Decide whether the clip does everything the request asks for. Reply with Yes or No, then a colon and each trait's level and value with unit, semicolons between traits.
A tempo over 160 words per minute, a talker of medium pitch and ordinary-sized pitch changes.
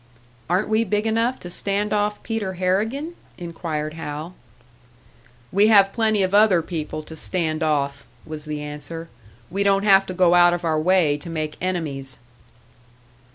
No: average, 155 wpm; medium, 180 Hz; average, 4.6 semitones